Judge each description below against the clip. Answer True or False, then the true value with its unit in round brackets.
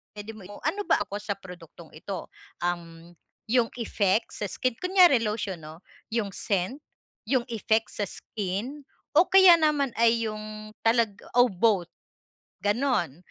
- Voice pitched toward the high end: True (215 Hz)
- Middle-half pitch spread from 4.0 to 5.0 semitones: True (4.6 semitones)